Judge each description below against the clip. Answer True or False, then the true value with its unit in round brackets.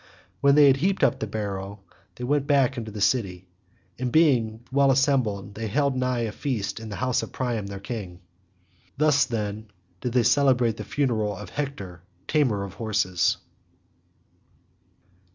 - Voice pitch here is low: True (120 Hz)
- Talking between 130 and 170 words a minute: True (160 wpm)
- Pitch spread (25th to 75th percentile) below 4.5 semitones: False (4.8 semitones)